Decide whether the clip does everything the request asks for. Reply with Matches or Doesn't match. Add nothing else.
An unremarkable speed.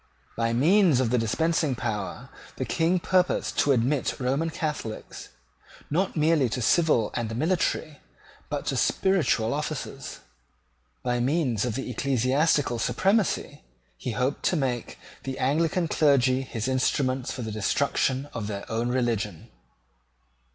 Doesn't match